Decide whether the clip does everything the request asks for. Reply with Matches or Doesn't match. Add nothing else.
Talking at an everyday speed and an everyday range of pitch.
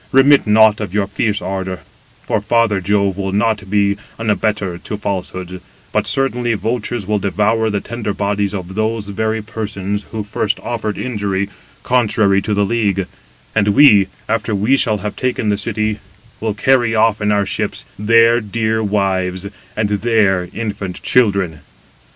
Doesn't match